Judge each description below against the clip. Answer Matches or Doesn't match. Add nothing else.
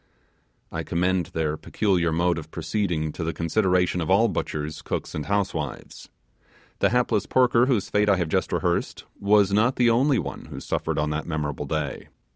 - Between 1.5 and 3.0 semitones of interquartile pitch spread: Doesn't match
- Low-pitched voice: Matches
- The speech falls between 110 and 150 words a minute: Doesn't match